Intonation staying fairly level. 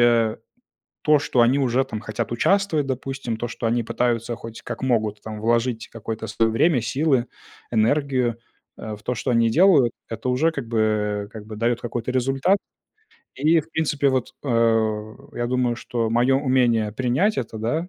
No: average, 3.0 semitones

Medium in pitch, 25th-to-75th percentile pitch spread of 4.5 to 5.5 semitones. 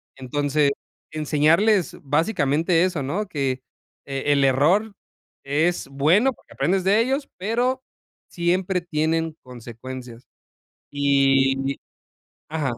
Yes: medium, 150 Hz; average, 5.0 semitones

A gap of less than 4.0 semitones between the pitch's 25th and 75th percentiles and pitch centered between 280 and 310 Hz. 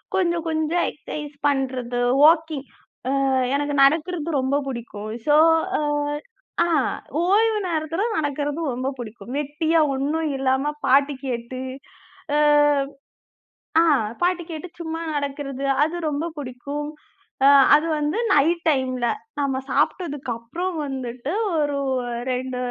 Yes: average, 3.4 semitones; very high, 290 Hz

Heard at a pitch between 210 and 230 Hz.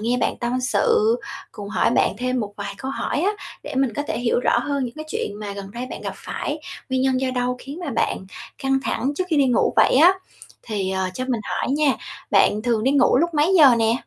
No: very high, 255 Hz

